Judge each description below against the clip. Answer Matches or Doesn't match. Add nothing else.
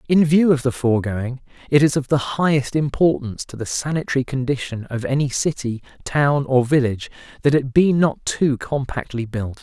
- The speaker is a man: Matches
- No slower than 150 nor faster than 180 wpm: Matches